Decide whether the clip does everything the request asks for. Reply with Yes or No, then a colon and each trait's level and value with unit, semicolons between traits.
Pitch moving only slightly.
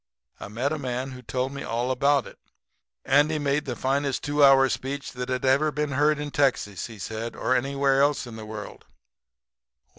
Yes: narrow, 2.2 semitones